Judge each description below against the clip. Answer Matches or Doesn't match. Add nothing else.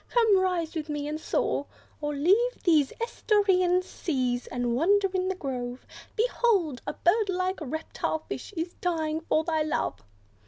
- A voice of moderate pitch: Doesn't match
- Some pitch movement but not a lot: Matches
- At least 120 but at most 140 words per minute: Doesn't match